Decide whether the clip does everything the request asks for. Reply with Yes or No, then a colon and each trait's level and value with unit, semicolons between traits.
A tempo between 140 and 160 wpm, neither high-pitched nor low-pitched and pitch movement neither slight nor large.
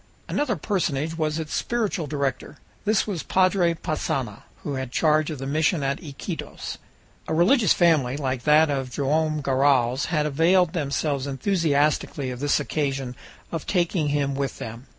Yes: average, 150 wpm; medium, 150 Hz; average, 3.3 semitones